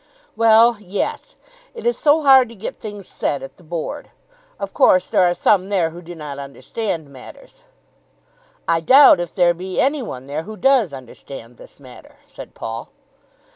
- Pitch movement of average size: No, wide, 7.3 semitones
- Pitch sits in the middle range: Yes, medium, 180 Hz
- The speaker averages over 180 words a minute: No, average, 175 wpm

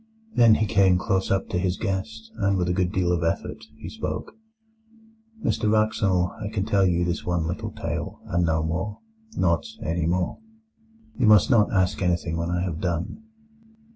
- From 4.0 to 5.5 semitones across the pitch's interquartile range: No, average, 3.3 semitones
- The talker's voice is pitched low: Yes, very low, 95 Hz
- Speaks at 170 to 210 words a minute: Yes, average, 175 wpm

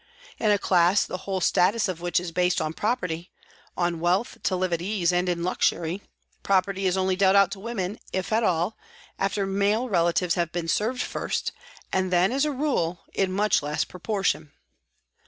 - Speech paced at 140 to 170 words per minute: No, average, 185 wpm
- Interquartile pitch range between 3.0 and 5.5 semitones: No, narrow, 2.5 semitones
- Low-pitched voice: No, medium, 185 Hz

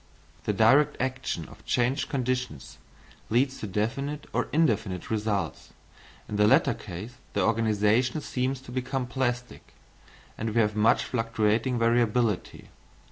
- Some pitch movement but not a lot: Yes, average, 3.2 semitones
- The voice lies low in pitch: Yes, low, 120 Hz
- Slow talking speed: Yes, slow, 130 wpm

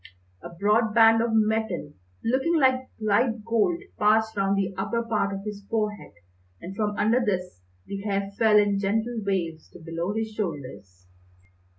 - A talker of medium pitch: No, high, 210 Hz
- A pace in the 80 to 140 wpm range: No, average, 160 wpm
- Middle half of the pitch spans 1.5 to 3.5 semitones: Yes, narrow, 2.4 semitones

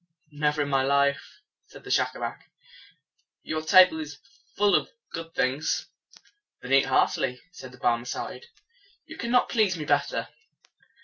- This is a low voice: No, medium, 150 Hz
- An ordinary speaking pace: No, slow, 130 wpm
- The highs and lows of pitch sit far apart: No, average, 4.3 semitones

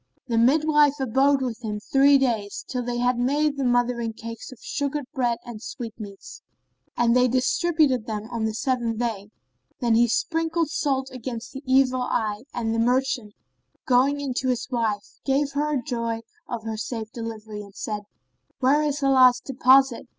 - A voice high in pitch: Yes, very high, 250 Hz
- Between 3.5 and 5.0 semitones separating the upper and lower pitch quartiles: No, average, 3.0 semitones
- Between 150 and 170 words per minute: Yes, average, 165 wpm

